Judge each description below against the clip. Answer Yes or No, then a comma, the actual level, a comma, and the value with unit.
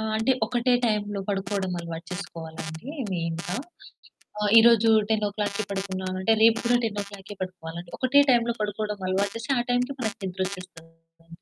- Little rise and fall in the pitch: No, average, 3.8 semitones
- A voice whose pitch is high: Yes, high, 200 Hz